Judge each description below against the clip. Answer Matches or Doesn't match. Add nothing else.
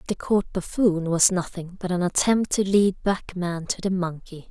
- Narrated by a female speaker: Matches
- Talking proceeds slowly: Doesn't match